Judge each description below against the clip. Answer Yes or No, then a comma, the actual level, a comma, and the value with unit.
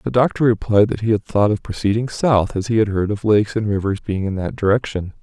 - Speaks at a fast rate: Yes, fast, 255 wpm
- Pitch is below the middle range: Yes, low, 105 Hz